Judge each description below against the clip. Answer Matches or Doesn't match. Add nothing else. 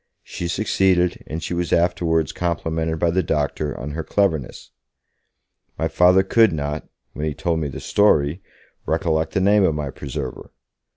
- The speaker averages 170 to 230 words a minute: Doesn't match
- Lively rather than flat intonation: Doesn't match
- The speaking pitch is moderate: Doesn't match